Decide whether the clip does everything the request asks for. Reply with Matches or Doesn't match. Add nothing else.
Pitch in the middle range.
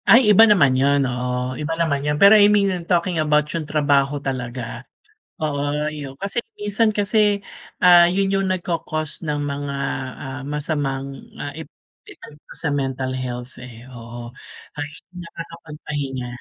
Matches